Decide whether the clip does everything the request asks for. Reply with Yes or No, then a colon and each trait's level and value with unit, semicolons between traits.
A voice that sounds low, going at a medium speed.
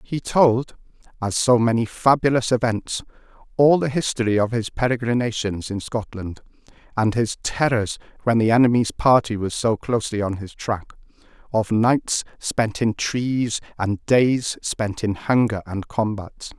Yes: low, 115 Hz; average, 145 wpm